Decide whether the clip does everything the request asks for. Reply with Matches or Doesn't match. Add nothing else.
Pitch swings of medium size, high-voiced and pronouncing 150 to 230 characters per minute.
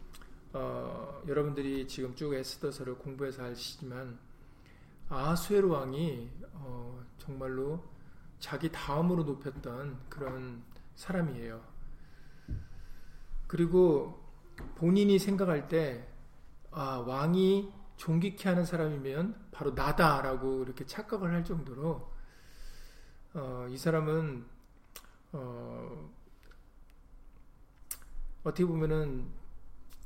Doesn't match